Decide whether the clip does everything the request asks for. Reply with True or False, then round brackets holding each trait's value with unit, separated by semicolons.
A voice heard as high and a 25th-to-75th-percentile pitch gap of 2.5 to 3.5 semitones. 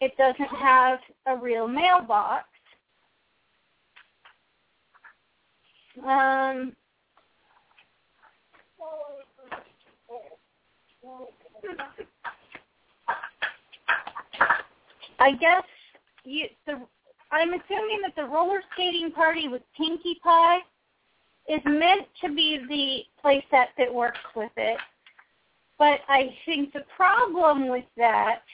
False (290 Hz; 4.5 semitones)